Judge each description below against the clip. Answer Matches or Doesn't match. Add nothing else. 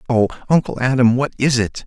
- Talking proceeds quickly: Doesn't match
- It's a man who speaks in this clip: Matches